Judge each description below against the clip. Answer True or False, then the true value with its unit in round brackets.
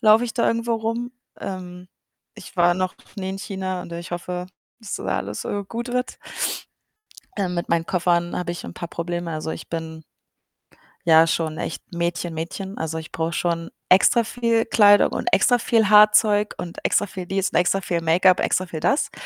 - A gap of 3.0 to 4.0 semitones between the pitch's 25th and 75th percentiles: True (3.6 semitones)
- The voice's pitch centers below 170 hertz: False (180 Hz)